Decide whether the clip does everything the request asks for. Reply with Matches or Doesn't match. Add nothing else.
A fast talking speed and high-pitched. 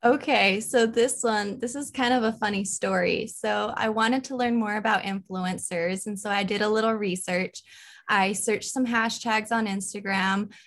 Doesn't match